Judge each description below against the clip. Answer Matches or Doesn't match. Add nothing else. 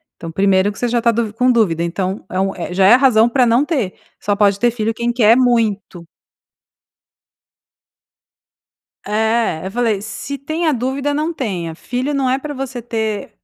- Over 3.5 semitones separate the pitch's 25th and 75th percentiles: Matches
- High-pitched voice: Matches